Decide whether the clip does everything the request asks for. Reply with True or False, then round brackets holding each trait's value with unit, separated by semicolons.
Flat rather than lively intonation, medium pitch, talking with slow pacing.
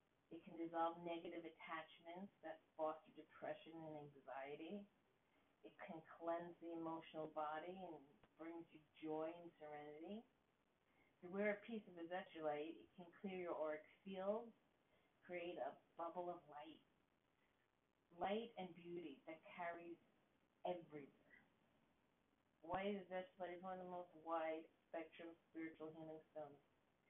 True (2.3 semitones; 165 Hz; 120 wpm)